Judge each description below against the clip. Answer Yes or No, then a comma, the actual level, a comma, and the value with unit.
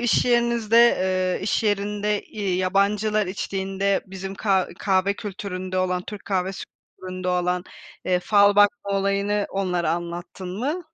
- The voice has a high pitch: Yes, high, 195 Hz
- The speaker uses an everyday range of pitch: No, narrow, 1.9 semitones